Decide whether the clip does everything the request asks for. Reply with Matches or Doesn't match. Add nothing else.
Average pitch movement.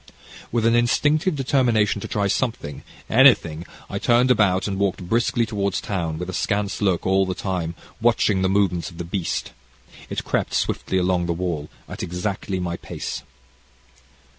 Matches